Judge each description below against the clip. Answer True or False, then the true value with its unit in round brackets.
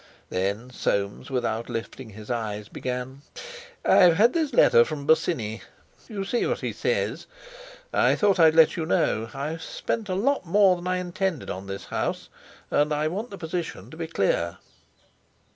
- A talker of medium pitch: True (155 Hz)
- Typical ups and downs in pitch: False (8.2 semitones)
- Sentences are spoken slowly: False (165 wpm)